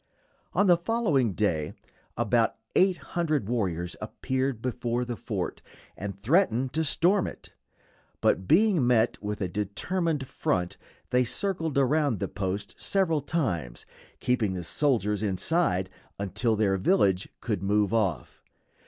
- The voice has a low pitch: Yes, low, 120 Hz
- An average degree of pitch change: No, wide, 7.8 semitones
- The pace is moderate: No, slow, 130 wpm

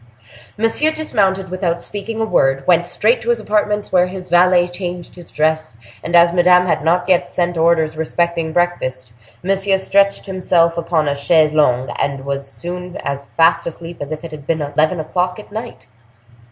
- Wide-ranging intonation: No, average, 3.0 semitones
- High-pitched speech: No, medium, 175 Hz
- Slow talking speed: No, average, 180 wpm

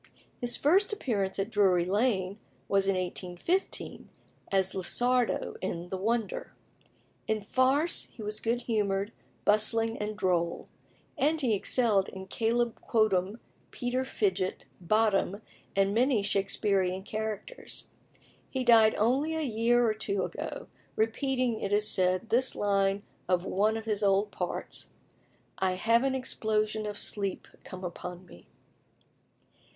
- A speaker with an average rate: No, slow, 130 wpm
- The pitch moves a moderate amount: Yes, average, 3.6 semitones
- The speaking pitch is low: No, high, 215 Hz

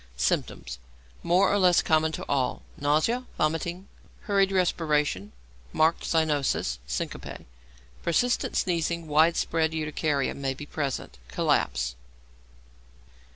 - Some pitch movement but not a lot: Yes, average, 3.2 semitones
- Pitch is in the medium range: Yes, medium, 155 Hz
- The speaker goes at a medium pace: No, slow, 105 wpm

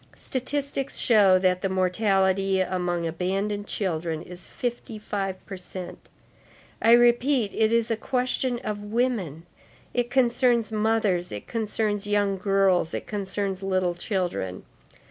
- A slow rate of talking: Yes, slow, 125 wpm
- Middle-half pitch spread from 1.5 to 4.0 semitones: Yes, average, 3.6 semitones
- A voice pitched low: No, high, 200 Hz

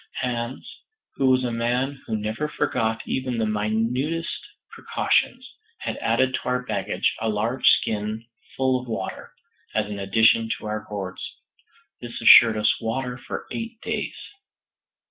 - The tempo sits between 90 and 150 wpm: Yes, average, 145 wpm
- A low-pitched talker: Yes, low, 115 Hz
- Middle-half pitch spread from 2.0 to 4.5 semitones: Yes, average, 3.2 semitones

